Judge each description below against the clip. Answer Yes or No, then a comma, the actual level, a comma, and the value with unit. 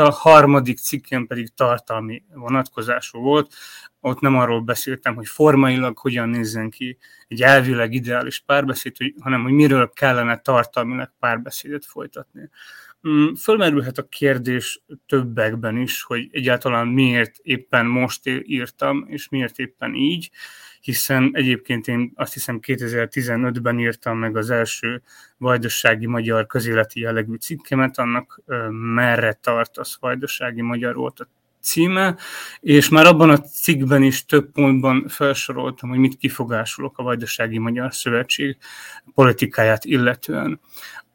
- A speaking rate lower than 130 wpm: Yes, average, 120 wpm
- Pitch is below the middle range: Yes, low, 125 Hz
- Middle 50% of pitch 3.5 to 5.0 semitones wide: No, narrow, 2.5 semitones